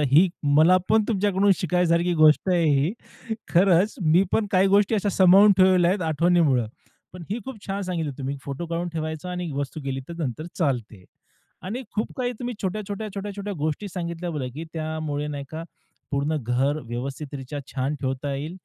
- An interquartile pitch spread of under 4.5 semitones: No, average, 4.8 semitones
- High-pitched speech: No, medium, 170 Hz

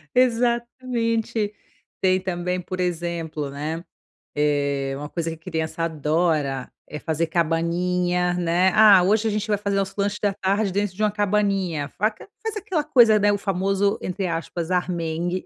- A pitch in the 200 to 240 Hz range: No, medium, 185 Hz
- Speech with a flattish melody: No, average, 3.8 semitones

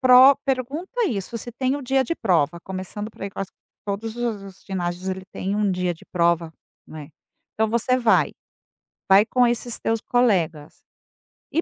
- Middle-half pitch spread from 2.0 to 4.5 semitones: No, average, 5.0 semitones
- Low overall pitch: No, high, 210 Hz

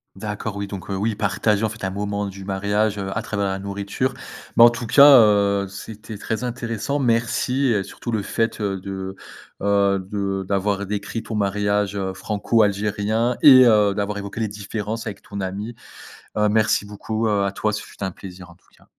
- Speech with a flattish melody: Yes, narrow, 1.9 semitones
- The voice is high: No, low, 105 Hz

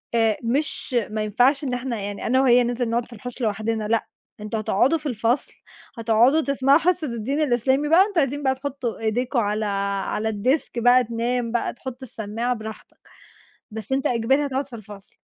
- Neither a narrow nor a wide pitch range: Yes, average, 3.3 semitones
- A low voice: No, high, 245 Hz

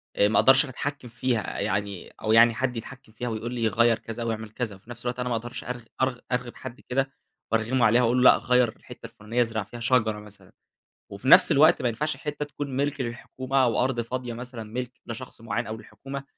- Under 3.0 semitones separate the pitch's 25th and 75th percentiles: Yes, narrow, 2.4 semitones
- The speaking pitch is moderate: No, low, 120 Hz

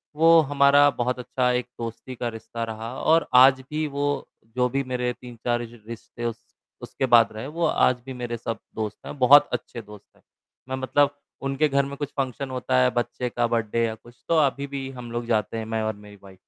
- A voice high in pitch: No, low, 125 Hz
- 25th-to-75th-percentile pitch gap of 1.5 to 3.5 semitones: Yes, average, 2.9 semitones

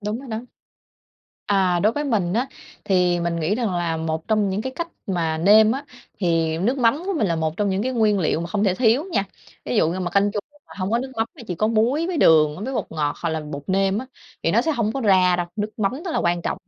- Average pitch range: Yes, average, 5.0 semitones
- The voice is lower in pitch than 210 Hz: Yes, high, 200 Hz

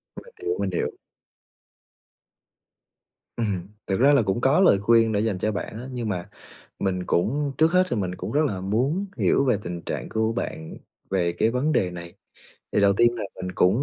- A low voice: Yes, low, 110 Hz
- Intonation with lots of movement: Yes, wide, 5.9 semitones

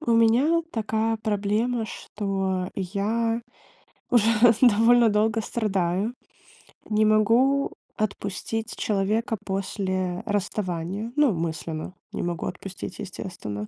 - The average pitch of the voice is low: No, high, 210 Hz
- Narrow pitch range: No, average, 3.2 semitones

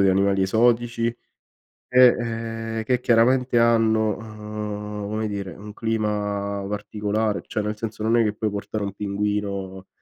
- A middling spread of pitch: No, narrow, 1.8 semitones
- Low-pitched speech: Yes, low, 105 Hz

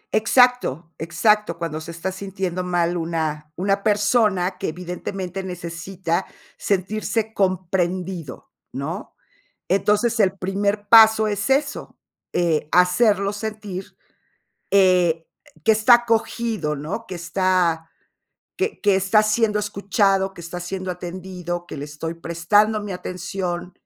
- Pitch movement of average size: Yes, average, 3.3 semitones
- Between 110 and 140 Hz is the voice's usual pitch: No, medium, 185 Hz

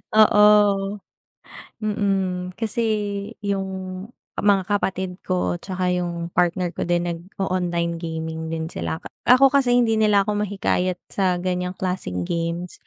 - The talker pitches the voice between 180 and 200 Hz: Yes, medium, 185 Hz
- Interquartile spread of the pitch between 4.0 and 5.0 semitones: No, average, 2.8 semitones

